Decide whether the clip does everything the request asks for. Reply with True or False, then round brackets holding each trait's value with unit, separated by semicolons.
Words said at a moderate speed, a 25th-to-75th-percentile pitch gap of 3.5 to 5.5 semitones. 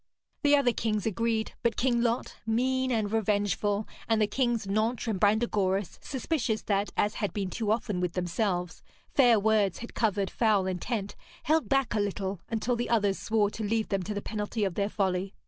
False (185 wpm; 2.7 semitones)